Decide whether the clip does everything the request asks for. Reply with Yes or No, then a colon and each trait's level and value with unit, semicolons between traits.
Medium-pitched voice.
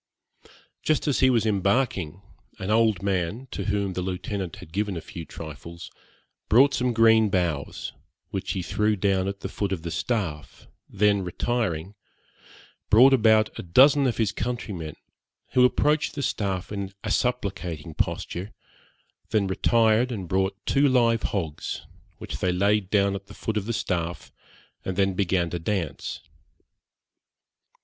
No: low, 100 Hz